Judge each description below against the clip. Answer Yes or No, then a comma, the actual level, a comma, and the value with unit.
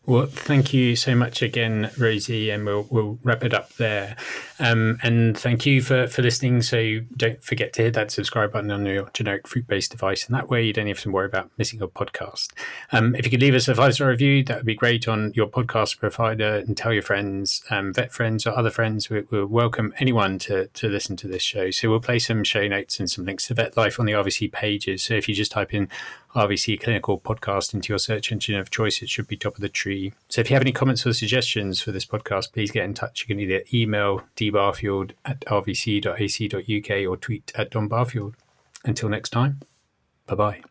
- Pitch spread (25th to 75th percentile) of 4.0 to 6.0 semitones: No, average, 2.9 semitones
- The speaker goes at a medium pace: No, fast, 230 wpm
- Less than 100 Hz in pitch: No, low, 110 Hz